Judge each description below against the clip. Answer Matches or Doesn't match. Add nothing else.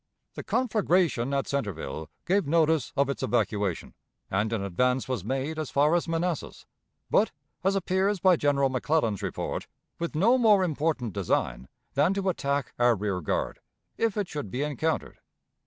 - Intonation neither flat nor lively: Doesn't match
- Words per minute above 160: Doesn't match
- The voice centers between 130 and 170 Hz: Matches